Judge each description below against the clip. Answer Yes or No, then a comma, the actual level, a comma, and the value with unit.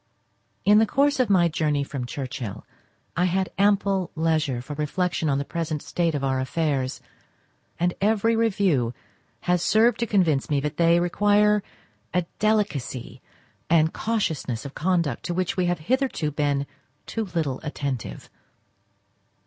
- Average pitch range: No, wide, 6.0 semitones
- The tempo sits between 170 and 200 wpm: No, average, 145 wpm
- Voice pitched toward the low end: No, medium, 165 Hz